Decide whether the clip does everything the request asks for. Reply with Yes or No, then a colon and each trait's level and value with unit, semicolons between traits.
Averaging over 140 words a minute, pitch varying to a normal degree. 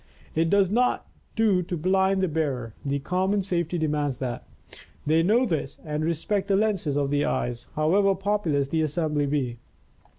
Yes: average, 165 wpm; average, 4.9 semitones